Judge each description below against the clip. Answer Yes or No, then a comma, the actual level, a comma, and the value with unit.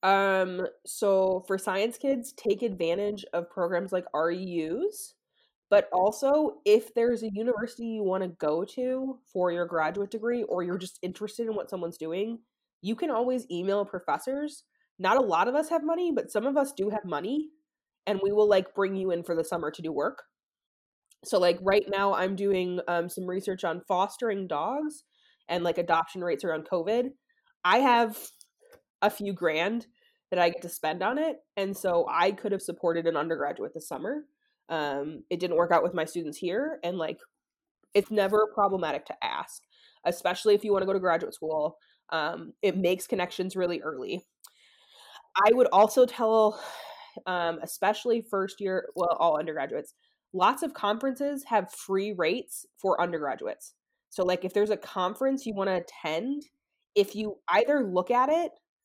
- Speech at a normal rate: Yes, average, 175 wpm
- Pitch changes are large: Yes, wide, 5.9 semitones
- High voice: Yes, high, 200 Hz